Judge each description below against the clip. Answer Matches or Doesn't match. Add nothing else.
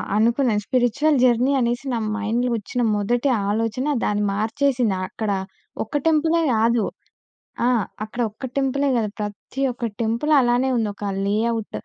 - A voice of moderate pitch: Doesn't match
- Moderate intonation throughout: Matches